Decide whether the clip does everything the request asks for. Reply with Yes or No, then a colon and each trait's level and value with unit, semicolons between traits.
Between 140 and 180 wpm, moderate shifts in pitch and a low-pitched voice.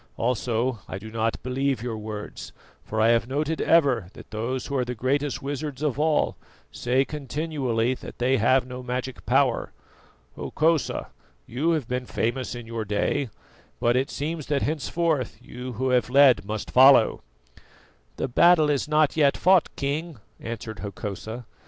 Yes: average, 160 wpm; average, 3.6 semitones; low, 130 Hz